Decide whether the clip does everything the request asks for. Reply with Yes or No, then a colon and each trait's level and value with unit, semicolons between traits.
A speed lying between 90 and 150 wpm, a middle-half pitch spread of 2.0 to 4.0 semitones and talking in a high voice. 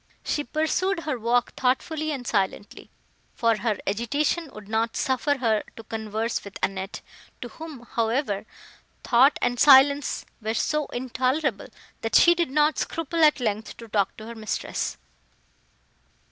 No: average, 145 wpm; average, 5.1 semitones; high, 245 Hz